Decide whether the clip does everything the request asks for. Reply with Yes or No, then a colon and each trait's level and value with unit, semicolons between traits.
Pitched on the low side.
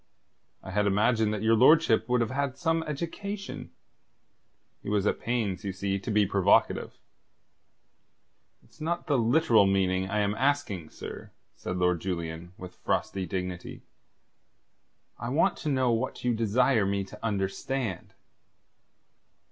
Yes: low, 110 Hz